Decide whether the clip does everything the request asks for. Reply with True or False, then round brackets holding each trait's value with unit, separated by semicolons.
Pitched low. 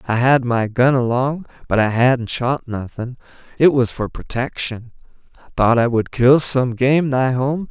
True (125 Hz)